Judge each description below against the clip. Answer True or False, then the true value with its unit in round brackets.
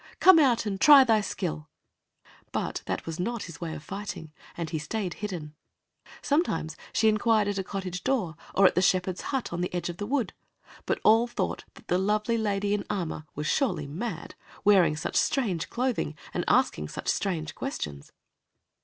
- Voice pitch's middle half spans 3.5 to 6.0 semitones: True (5.3 semitones)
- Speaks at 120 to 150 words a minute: False (180 wpm)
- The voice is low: False (195 Hz)